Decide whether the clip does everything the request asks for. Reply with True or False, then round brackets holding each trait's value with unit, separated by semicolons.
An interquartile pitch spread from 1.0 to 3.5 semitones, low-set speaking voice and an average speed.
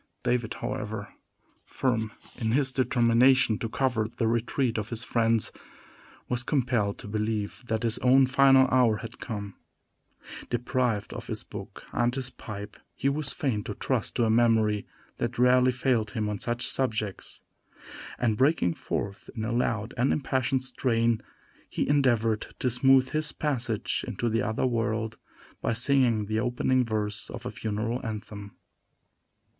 True (2.8 semitones; 115 Hz; 150 wpm)